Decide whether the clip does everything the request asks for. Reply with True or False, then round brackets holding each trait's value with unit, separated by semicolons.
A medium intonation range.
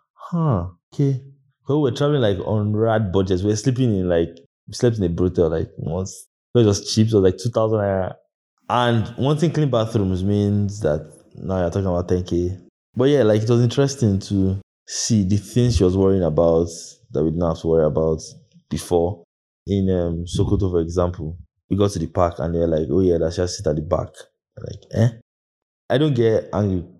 True (4.6 semitones)